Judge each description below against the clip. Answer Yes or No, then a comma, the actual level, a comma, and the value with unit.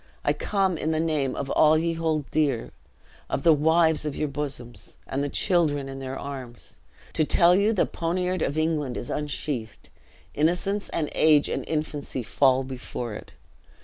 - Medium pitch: Yes, medium, 150 Hz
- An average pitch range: Yes, average, 3.4 semitones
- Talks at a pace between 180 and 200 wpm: No, average, 170 wpm